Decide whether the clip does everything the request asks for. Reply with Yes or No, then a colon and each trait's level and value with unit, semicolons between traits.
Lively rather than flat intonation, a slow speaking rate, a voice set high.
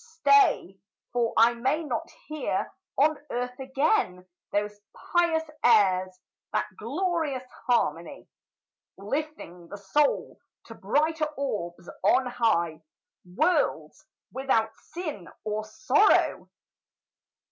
Yes: wide, 6.8 semitones; slow, 95 wpm; very high, 250 Hz